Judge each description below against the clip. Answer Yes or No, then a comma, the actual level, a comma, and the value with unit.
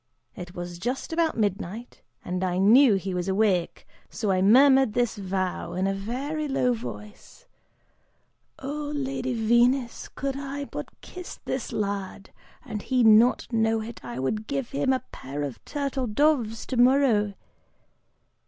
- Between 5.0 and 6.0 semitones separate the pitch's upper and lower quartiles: Yes, wide, 5.4 semitones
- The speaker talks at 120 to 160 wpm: Yes, average, 145 wpm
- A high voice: Yes, high, 225 Hz